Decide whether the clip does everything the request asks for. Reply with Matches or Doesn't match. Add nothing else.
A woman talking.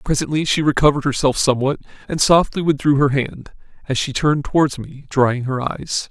Doesn't match